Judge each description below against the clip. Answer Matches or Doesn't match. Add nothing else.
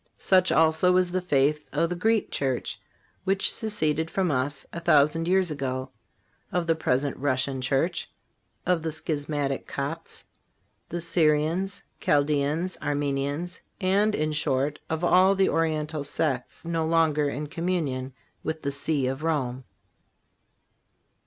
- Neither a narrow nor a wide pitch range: Matches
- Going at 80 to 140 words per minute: Matches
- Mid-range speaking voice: Matches